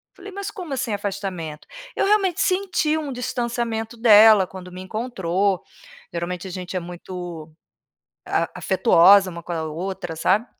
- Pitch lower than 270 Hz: Yes, high, 200 Hz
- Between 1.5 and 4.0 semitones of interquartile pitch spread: No, wide, 5.5 semitones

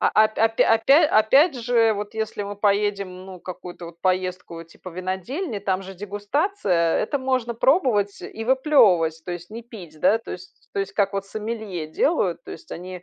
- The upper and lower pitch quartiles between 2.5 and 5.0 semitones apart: Yes, average, 4.0 semitones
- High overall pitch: Yes, high, 205 Hz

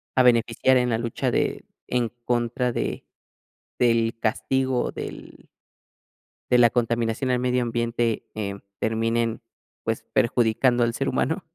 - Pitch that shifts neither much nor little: No, narrow, 1.4 semitones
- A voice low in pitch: Yes, low, 120 Hz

